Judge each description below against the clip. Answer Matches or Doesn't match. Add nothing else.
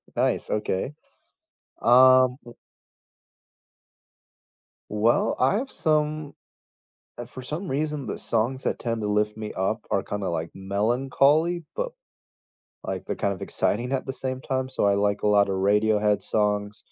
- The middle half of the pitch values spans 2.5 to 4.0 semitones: Doesn't match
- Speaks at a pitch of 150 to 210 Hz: Doesn't match